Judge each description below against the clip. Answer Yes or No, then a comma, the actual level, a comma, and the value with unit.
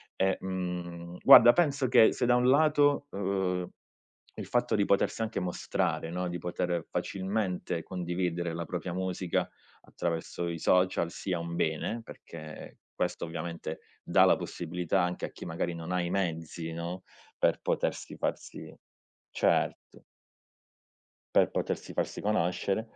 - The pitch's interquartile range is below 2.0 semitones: No, narrow, 2.4 semitones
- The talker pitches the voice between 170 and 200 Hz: No, very low, 90 Hz